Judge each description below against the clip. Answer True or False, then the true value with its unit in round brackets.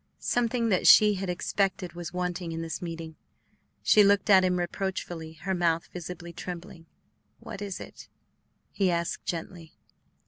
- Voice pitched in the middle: True (180 Hz)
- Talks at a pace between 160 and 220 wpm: False (145 wpm)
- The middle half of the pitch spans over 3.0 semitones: False (2.4 semitones)